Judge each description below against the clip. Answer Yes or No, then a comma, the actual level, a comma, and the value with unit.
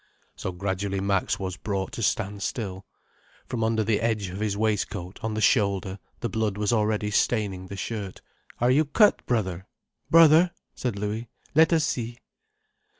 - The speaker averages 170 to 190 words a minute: No, average, 160 wpm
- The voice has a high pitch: No, low, 105 Hz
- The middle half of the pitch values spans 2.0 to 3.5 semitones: Yes, average, 3.0 semitones